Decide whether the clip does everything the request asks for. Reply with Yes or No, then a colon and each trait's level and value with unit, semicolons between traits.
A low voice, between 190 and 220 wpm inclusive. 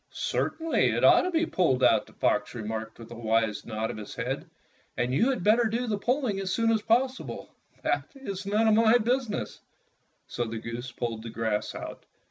No: high, 190 Hz; average, 195 wpm